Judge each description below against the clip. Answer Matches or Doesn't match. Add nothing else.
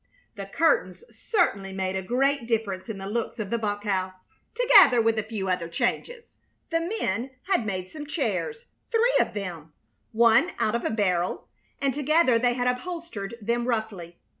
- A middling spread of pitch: Doesn't match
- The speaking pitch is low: Doesn't match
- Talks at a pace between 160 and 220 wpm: Matches